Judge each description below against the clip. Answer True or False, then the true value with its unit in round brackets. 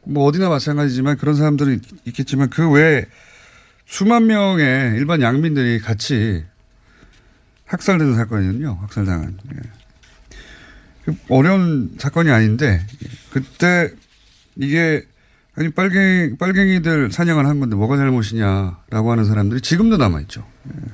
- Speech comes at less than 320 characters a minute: True (280 characters per minute)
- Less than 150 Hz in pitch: True (135 Hz)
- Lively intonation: True (6.2 semitones)